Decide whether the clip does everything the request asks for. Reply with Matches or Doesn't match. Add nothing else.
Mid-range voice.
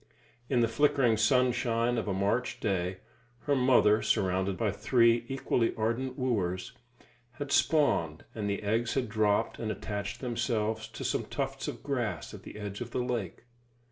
Doesn't match